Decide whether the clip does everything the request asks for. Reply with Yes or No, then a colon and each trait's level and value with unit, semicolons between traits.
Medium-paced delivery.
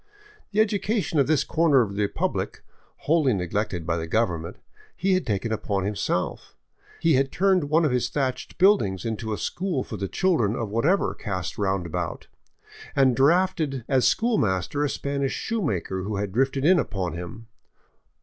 Yes: average, 160 wpm